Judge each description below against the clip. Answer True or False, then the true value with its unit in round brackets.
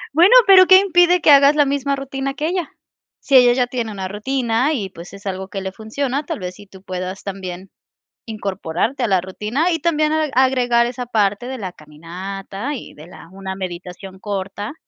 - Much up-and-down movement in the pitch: True (6.5 semitones)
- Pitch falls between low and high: False (220 Hz)